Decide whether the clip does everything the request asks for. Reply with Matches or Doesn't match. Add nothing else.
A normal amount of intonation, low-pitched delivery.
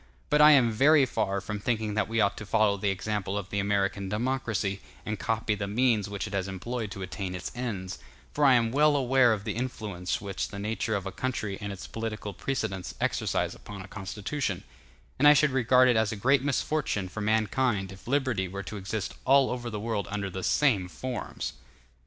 Matches